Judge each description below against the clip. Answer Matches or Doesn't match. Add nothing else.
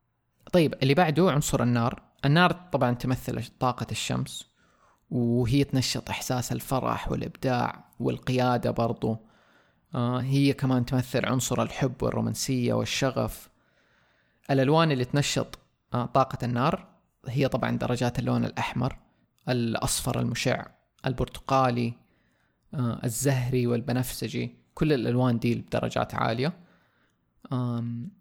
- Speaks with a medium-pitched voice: Doesn't match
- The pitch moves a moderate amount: Doesn't match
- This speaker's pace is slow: Doesn't match